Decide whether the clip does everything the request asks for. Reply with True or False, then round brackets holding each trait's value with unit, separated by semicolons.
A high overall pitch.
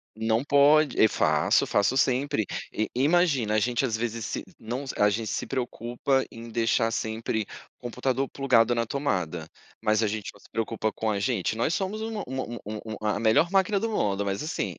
False (115 Hz)